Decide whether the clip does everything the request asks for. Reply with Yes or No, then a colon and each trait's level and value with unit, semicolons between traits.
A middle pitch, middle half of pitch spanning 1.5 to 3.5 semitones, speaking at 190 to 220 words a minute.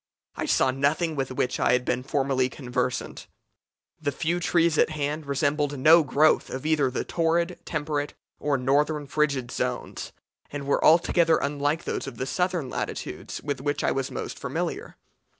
No: medium, 145 Hz; average, 2.7 semitones; average, 165 wpm